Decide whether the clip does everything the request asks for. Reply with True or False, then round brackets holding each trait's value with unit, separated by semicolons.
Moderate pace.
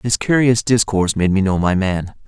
False (210 wpm)